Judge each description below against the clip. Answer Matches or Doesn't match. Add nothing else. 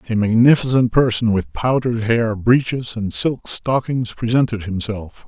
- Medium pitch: Doesn't match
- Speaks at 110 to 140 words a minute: Matches